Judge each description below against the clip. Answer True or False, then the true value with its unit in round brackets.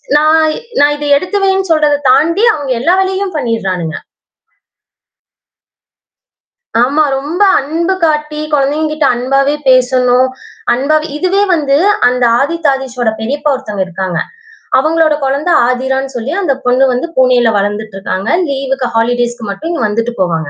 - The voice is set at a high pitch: True (270 Hz)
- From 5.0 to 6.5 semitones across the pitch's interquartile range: False (4.1 semitones)